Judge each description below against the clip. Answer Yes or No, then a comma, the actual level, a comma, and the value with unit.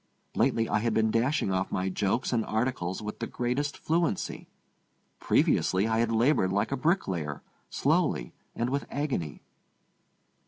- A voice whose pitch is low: Yes, low, 115 Hz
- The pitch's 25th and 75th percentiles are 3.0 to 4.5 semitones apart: No, average, 5.1 semitones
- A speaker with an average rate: Yes, average, 145 wpm